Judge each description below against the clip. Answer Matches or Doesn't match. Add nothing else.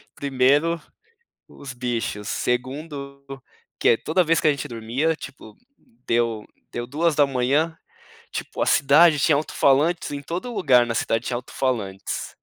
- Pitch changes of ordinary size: Matches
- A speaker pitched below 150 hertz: Matches